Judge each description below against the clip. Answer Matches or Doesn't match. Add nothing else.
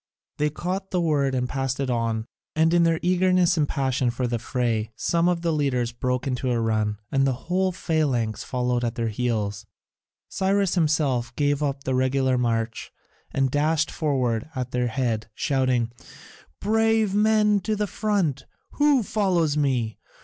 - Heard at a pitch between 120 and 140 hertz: Matches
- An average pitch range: Doesn't match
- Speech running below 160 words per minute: Doesn't match